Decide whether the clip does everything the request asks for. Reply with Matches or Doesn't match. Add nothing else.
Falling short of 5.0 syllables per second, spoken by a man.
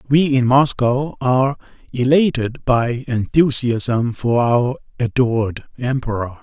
Matches